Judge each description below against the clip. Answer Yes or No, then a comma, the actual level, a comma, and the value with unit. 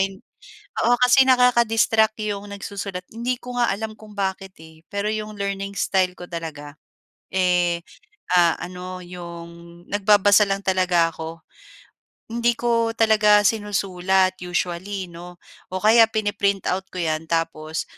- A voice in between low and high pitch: No, high, 195 Hz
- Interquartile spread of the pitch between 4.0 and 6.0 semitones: No, average, 3.3 semitones